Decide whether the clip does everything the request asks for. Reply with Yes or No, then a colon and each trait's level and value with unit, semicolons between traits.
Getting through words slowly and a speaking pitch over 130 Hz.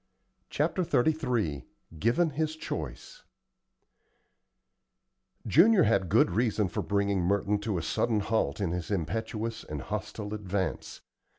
No: slow, 115 wpm; low, 105 Hz